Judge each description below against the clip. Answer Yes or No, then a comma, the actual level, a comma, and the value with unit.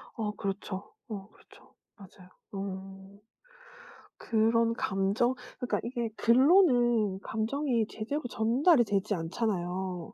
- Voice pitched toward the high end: Yes, high, 215 Hz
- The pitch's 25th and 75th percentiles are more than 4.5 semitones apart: No, average, 3.6 semitones